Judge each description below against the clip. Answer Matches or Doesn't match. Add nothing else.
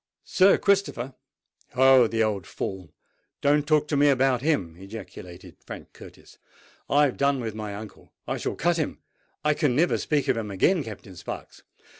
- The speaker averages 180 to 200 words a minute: Doesn't match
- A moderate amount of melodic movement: Doesn't match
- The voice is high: Doesn't match